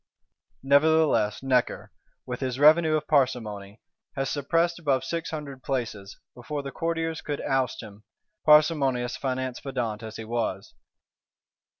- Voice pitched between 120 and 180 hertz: Yes, low, 135 Hz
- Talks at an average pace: No, slow, 125 wpm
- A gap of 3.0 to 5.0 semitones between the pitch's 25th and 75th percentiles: Yes, average, 4.2 semitones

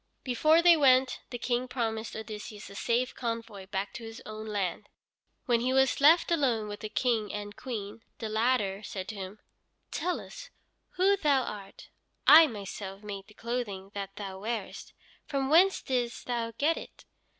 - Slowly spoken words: No, average, 170 wpm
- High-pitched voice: Yes, high, 230 Hz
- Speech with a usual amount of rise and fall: Yes, average, 4.0 semitones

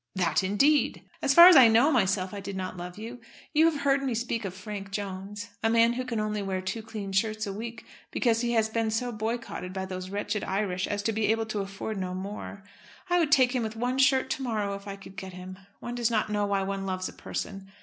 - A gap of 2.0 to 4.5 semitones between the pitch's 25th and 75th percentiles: Yes, average, 3.3 semitones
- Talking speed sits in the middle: No, fast, 245 wpm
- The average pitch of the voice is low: No, high, 210 Hz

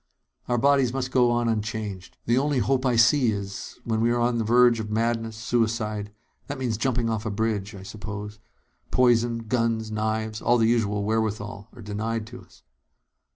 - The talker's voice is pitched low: Yes, low, 115 Hz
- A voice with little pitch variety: Yes, narrow, 2.0 semitones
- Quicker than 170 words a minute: Yes, average, 180 wpm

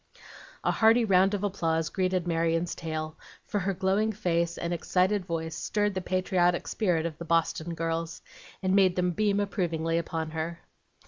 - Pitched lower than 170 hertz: No, medium, 175 Hz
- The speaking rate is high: No, average, 165 wpm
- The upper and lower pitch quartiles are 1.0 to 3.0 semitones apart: Yes, average, 2.7 semitones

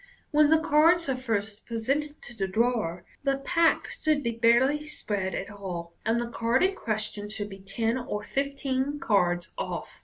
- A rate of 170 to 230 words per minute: Yes, average, 175 wpm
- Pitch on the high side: Yes, high, 235 Hz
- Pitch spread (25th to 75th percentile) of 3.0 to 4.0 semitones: No, wide, 5.5 semitones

